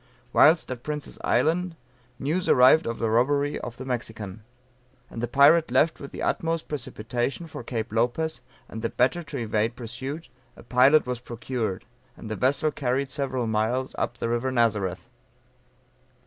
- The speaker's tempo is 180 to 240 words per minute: No, average, 160 wpm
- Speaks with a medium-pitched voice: No, low, 125 Hz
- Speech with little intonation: No, average, 3.9 semitones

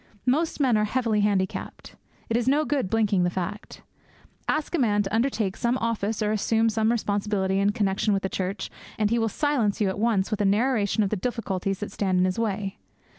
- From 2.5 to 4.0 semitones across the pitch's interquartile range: Yes, average, 2.9 semitones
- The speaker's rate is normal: No, fast, 210 wpm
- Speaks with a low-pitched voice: No, high, 210 Hz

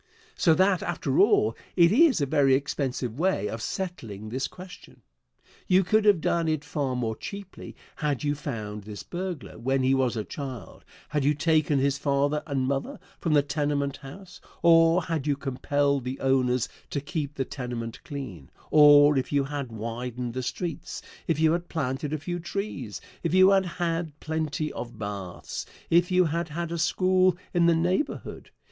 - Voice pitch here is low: No, medium, 145 Hz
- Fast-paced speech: No, average, 175 wpm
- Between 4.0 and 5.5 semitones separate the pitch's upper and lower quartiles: Yes, average, 4.5 semitones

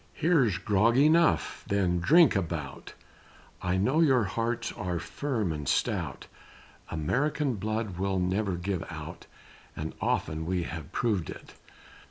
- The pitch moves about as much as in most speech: No, wide, 5.8 semitones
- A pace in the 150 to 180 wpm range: No, slow, 135 wpm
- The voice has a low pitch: Yes, low, 100 Hz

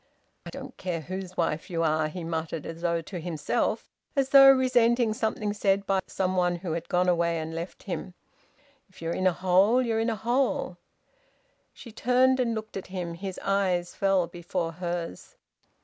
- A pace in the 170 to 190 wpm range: Yes, average, 180 wpm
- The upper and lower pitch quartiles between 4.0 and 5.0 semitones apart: Yes, average, 4.6 semitones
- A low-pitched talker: No, medium, 185 Hz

